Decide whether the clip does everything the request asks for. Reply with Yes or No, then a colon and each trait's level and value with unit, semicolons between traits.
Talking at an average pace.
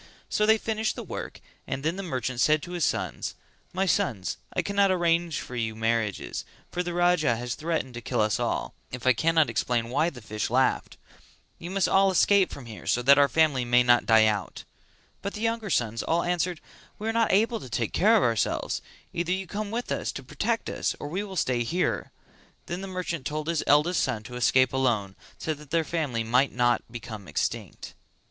No: fast, 210 wpm